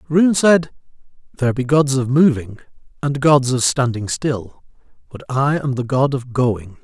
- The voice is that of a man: Yes, male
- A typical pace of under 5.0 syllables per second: Yes, 4.4 syllables/s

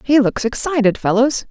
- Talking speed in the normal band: Yes, average, 160 wpm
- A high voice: Yes, high, 245 Hz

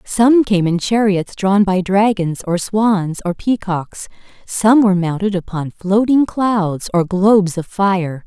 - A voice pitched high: Yes, high, 195 Hz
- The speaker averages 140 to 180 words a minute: Yes, average, 150 wpm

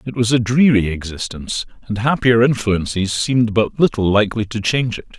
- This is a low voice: Yes, low, 110 Hz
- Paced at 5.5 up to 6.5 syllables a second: Yes, 5.6 syllables/s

